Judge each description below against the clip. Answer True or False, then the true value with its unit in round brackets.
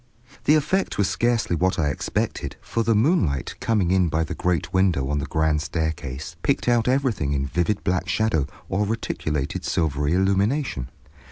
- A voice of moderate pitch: False (90 Hz)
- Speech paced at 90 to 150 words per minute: False (165 wpm)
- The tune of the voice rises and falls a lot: True (6.7 semitones)